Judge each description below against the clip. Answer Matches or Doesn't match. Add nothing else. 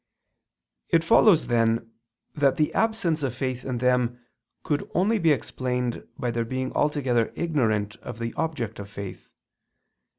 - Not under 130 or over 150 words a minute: Matches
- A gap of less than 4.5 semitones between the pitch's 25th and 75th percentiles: Doesn't match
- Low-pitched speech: Matches